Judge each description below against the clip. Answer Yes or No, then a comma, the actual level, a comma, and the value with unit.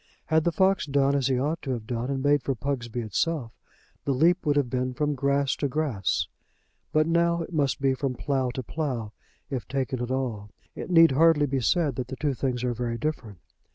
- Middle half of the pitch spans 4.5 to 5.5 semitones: No, average, 3.4 semitones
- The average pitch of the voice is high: No, low, 135 Hz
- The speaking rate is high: Yes, fast, 215 wpm